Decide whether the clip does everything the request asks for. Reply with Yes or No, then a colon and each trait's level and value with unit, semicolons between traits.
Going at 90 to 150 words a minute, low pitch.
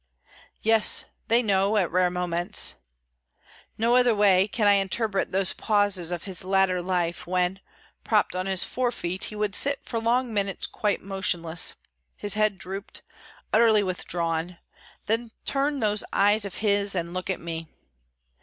No: average, 145 wpm; high, 195 Hz